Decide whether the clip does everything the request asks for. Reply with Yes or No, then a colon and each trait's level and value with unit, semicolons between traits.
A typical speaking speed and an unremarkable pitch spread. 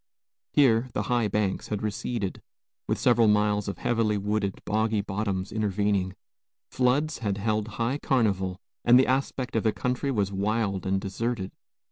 Yes: average, 150 wpm; average, 3.1 semitones